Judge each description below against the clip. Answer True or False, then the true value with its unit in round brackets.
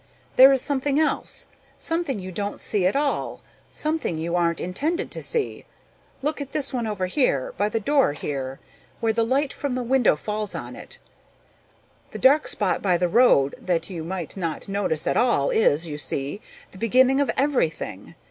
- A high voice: True (210 Hz)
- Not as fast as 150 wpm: False (180 wpm)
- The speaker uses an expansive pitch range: True (7.9 semitones)